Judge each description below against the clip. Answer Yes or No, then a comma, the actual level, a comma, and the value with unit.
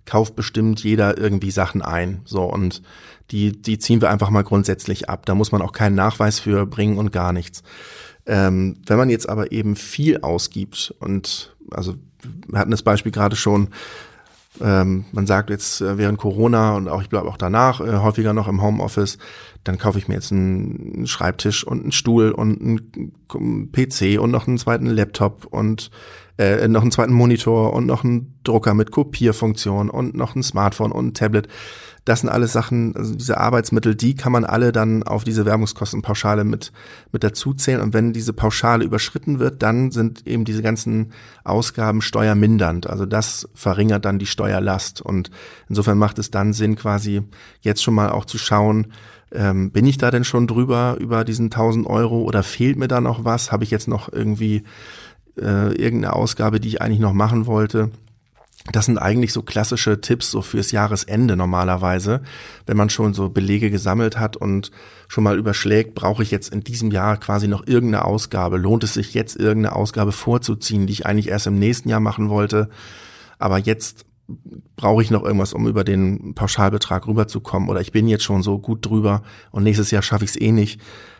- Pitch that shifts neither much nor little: No, narrow, 2.0 semitones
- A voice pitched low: Yes, low, 105 Hz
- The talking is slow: No, average, 185 wpm